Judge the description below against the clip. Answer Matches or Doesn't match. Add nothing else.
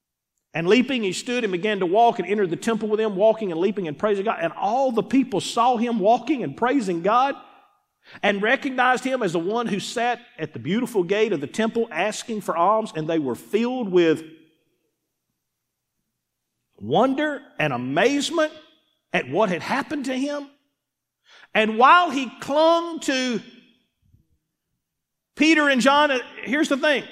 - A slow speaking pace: Doesn't match